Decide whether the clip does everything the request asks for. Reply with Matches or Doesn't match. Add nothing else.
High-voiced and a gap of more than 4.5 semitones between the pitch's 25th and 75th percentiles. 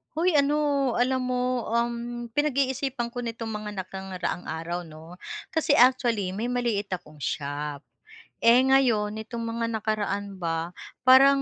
Matches